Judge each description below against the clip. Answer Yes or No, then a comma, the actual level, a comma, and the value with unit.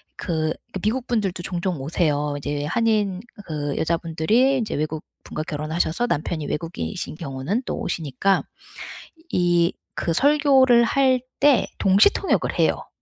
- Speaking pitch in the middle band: Yes, medium, 175 Hz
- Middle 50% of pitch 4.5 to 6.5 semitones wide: No, wide, 7.0 semitones